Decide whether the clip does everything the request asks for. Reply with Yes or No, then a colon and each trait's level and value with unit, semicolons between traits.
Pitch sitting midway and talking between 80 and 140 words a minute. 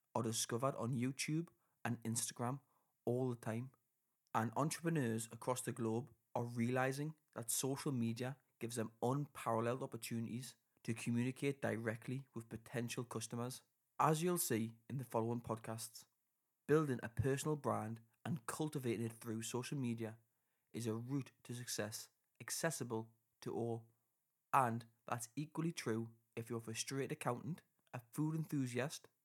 No: low, 120 Hz; slow, 135 wpm